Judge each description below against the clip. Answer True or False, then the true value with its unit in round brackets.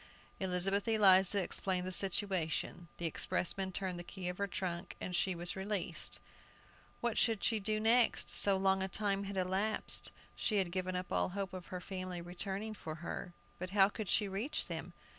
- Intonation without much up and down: True (2.0 semitones)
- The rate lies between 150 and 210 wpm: True (180 wpm)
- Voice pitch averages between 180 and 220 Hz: True (190 Hz)